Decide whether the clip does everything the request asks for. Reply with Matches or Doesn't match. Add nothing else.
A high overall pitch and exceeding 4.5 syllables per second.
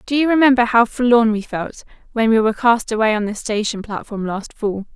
Matches